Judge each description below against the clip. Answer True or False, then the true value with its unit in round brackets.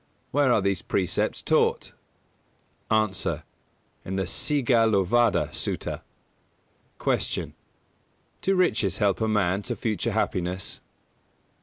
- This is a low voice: True (105 Hz)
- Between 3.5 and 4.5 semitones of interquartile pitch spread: True (3.8 semitones)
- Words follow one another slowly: True (105 wpm)